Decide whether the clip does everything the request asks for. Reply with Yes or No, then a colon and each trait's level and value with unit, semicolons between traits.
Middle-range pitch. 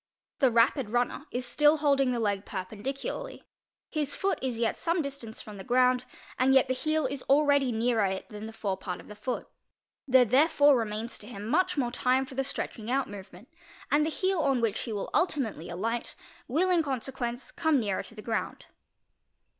No: very high, 250 Hz